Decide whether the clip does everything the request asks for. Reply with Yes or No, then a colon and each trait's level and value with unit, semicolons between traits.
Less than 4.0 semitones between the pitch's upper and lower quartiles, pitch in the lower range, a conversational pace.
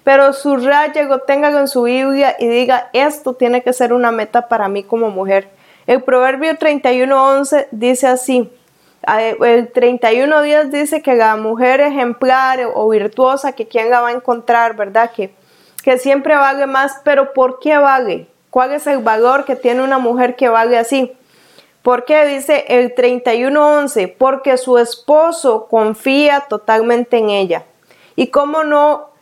No: average, 2.7 semitones; very high, 255 Hz; average, 155 wpm